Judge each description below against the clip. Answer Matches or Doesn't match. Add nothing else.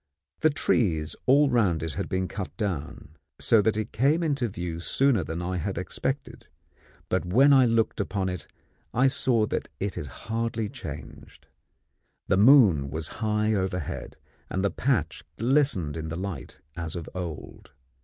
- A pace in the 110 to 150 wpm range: Doesn't match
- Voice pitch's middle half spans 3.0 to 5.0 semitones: Doesn't match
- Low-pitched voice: Matches